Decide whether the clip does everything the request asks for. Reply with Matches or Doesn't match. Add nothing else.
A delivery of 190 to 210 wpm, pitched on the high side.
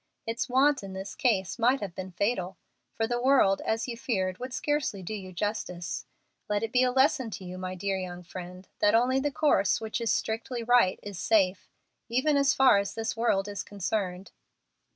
Matches